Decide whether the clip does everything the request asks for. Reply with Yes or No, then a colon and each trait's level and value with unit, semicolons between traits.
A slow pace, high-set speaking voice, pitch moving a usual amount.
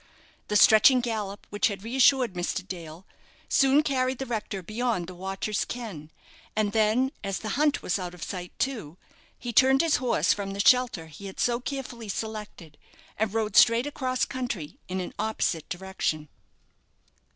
No: average, 165 wpm; high, 215 Hz; average, 4.9 semitones